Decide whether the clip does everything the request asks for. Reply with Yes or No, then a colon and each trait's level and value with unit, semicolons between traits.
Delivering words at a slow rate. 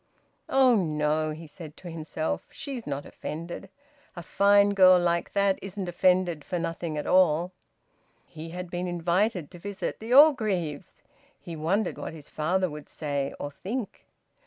No: average, 155 wpm